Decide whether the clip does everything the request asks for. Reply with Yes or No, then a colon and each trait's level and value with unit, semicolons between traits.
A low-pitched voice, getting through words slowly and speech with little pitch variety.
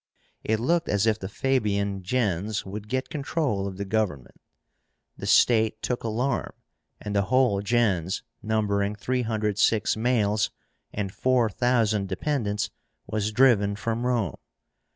No: low, 110 Hz; slow, 125 wpm; average, 3.3 semitones